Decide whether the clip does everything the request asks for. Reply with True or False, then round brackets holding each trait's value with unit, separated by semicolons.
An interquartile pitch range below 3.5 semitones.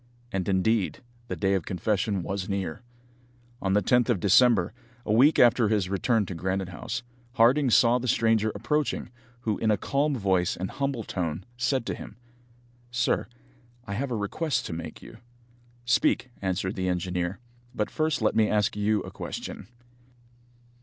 False (4.2 semitones)